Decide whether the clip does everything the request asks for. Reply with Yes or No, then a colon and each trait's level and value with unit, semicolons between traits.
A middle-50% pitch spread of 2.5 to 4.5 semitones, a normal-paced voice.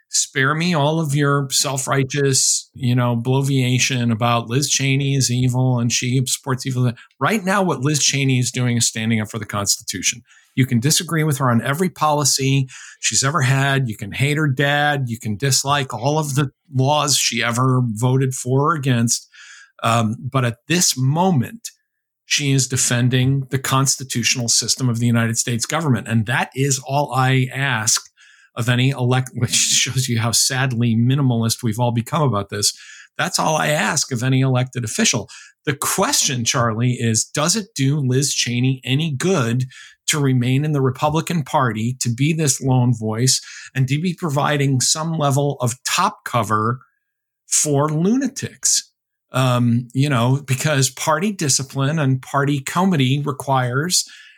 Yes: average, 3.0 semitones; average, 165 wpm